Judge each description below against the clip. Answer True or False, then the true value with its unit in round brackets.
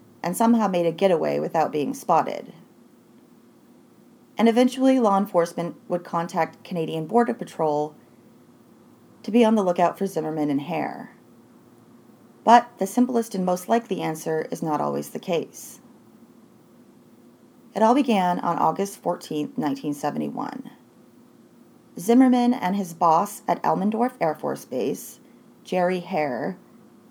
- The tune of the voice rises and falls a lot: True (6.4 semitones)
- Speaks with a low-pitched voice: False (185 Hz)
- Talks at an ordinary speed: False (125 wpm)